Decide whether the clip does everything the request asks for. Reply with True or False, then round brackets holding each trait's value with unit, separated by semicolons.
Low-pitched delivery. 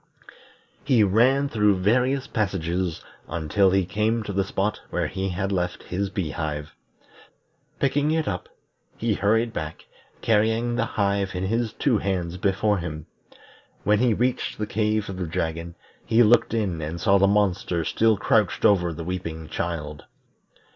True (100 Hz)